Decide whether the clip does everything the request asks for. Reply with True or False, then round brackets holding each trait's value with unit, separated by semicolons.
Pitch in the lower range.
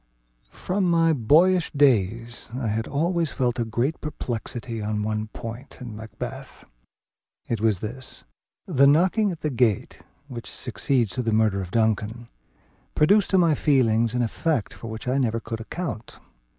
True (120 Hz)